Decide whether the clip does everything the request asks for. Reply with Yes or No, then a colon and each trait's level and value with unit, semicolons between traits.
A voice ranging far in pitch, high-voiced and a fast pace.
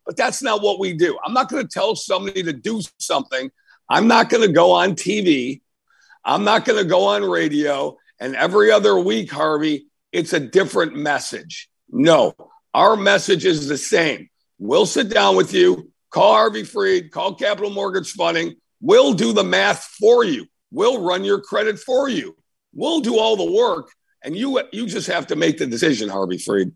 No: wide, 8.1 semitones; high, 205 Hz; average, 190 wpm